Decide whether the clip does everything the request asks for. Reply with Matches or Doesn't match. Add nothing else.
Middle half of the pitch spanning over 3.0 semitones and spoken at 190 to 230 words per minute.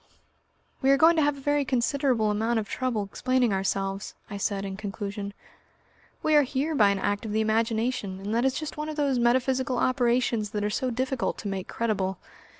Matches